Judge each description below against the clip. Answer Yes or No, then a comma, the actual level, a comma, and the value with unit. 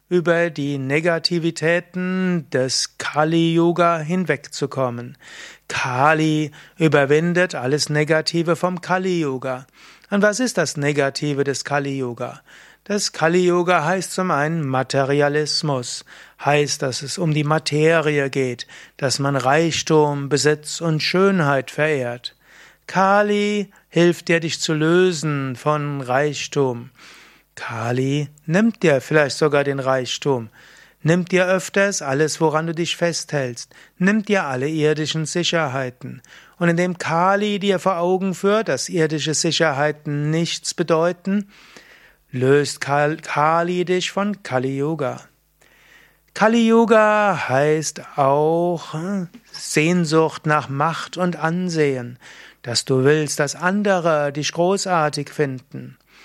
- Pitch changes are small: No, average, 3.8 semitones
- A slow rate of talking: Yes, slow, 115 wpm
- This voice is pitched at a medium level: Yes, medium, 155 Hz